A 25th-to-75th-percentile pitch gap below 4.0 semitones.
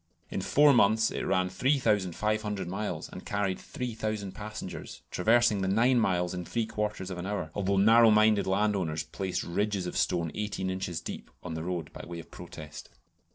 Yes: average, 3.1 semitones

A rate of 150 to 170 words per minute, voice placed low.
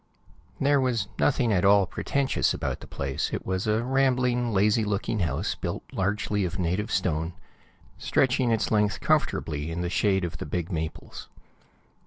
Yes: average, 160 wpm; low, 100 Hz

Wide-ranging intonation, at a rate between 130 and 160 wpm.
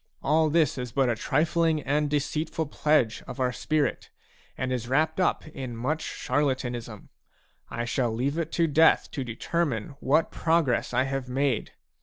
No: average, 3.8 semitones; average, 155 wpm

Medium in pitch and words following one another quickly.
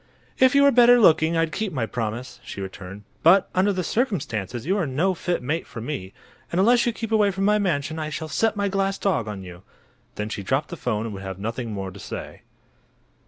Yes: medium, 155 Hz; fast, 225 wpm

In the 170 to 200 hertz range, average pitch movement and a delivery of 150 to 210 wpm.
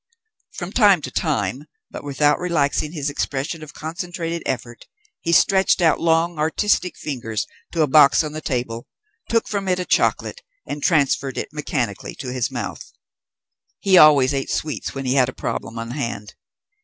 No: medium, 150 Hz; average, 4.3 semitones; average, 165 wpm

